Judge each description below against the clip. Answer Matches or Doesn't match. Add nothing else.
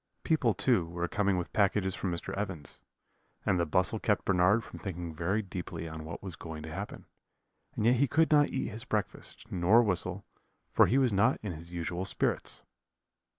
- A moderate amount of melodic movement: Matches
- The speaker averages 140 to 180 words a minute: Doesn't match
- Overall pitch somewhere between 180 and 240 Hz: Doesn't match